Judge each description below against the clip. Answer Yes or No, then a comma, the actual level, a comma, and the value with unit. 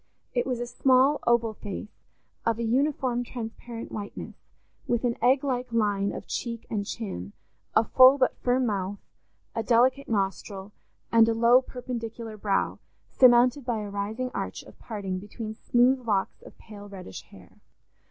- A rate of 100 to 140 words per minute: No, average, 155 wpm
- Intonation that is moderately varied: Yes, average, 3.2 semitones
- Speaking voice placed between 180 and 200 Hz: No, high, 230 Hz